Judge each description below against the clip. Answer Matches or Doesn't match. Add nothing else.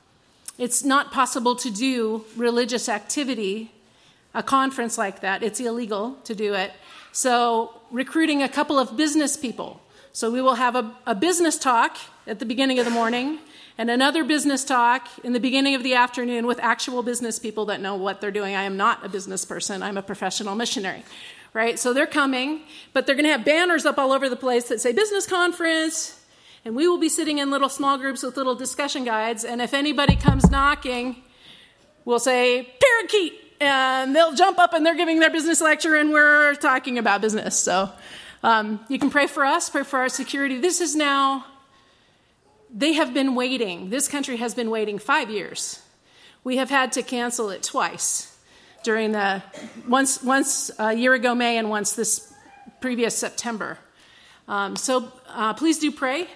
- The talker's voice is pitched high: Matches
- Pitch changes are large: Doesn't match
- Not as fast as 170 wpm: Doesn't match